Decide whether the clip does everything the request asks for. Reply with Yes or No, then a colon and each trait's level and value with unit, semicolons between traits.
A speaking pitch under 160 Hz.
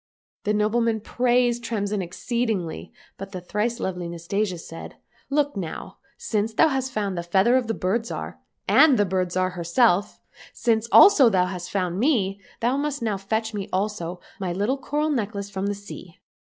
No: high, 205 Hz